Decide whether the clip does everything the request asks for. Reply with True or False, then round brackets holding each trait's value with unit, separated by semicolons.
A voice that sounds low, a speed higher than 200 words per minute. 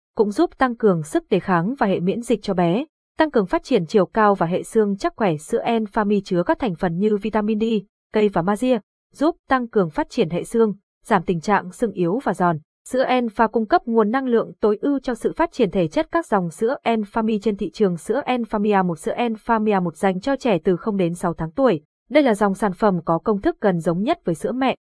False (215 Hz; 245 wpm)